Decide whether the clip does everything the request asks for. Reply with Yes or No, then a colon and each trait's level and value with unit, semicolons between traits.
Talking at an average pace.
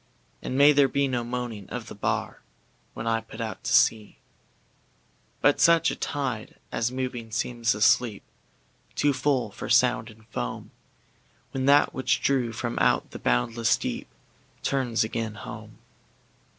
No: slow, 130 wpm